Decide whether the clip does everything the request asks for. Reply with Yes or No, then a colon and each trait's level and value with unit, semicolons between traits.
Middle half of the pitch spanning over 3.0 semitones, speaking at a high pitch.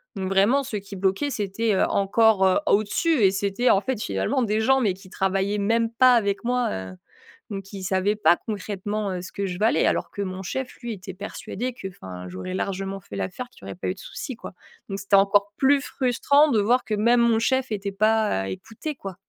Yes: average, 3.4 semitones; high, 205 Hz